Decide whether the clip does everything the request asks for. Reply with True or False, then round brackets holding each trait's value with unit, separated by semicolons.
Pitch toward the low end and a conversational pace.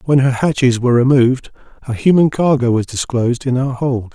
True (130 Hz; 190 wpm)